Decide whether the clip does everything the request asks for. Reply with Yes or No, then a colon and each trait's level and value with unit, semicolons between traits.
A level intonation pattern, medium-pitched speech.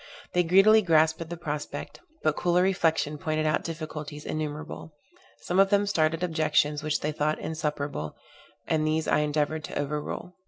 Yes: narrow, 2.1 semitones; medium, 155 Hz